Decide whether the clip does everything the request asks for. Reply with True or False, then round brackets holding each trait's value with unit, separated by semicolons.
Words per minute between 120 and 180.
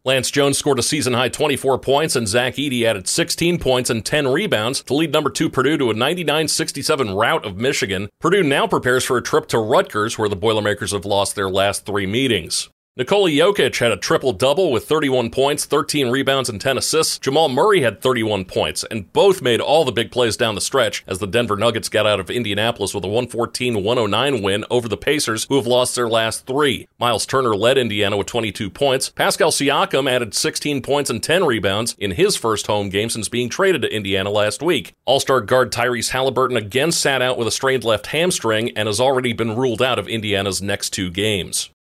False (205 wpm)